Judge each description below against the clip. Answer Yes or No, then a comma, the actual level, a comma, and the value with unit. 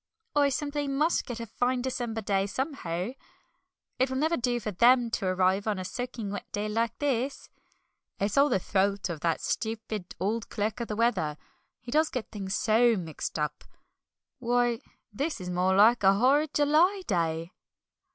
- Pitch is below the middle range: No, high, 225 Hz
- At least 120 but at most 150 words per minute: No, average, 170 wpm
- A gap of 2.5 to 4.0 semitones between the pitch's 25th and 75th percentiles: No, average, 5.0 semitones